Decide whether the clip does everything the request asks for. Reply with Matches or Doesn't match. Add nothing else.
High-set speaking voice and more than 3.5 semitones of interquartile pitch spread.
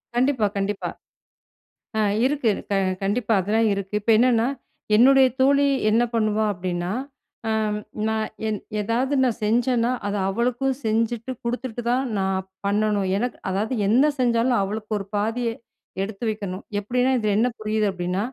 Doesn't match